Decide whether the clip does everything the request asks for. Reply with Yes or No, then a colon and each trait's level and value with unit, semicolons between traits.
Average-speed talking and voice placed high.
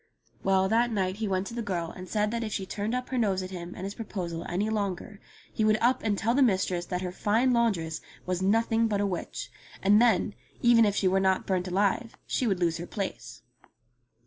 No: fast, 225 wpm; high, 200 Hz